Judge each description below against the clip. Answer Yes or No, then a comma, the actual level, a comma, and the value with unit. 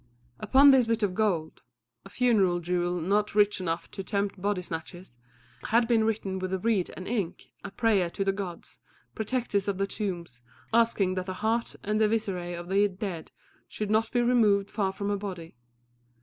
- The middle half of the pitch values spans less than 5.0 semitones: Yes, average, 3.1 semitones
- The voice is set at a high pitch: Yes, high, 200 Hz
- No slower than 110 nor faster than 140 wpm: No, average, 185 wpm